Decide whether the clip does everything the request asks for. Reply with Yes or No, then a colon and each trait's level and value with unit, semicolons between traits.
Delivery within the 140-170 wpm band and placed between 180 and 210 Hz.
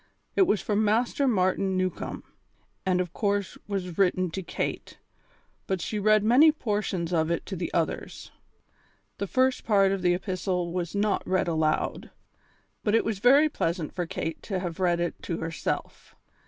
Yes: average, 165 wpm; high, 190 Hz